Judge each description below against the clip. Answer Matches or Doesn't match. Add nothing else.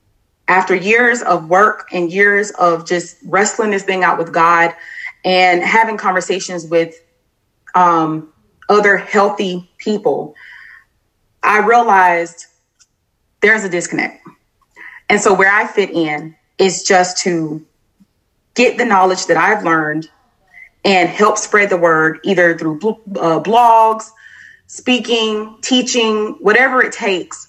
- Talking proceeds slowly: Matches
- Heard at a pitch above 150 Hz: Matches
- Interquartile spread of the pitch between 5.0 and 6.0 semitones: Doesn't match